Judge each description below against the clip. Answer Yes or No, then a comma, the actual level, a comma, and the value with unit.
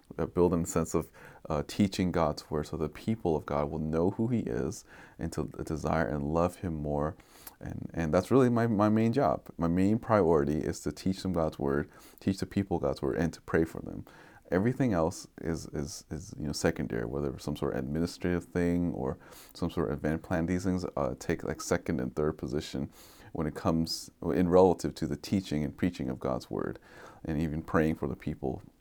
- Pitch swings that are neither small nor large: Yes, average, 3.5 semitones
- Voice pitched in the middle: No, very low, 80 Hz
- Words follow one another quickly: Yes, fast, 210 wpm